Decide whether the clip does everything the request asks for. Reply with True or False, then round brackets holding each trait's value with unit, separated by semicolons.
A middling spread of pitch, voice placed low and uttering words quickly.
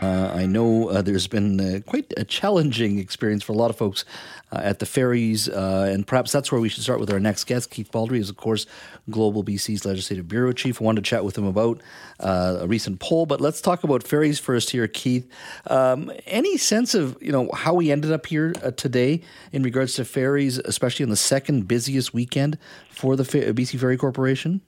True (4.8 semitones; 125 Hz; 220 wpm)